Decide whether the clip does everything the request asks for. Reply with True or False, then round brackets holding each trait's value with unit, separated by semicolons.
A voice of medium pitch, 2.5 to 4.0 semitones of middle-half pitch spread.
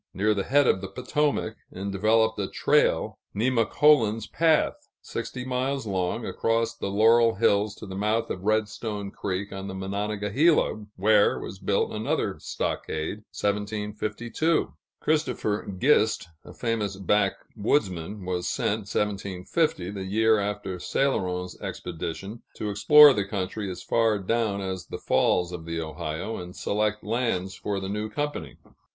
False (105 Hz; 2.9 semitones)